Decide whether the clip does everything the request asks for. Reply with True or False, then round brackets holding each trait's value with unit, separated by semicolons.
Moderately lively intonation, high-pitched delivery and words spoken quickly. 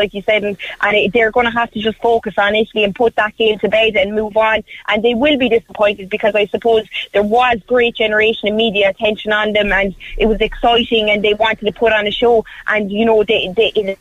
False (1.5 semitones; 215 Hz; 255 wpm)